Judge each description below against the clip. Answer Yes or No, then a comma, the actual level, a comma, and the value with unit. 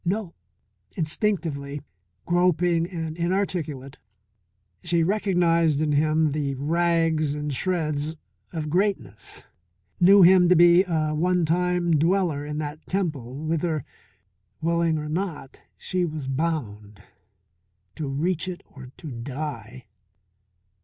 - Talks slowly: Yes, slow, 110 wpm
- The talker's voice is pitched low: No, medium, 160 Hz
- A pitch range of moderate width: Yes, average, 3.1 semitones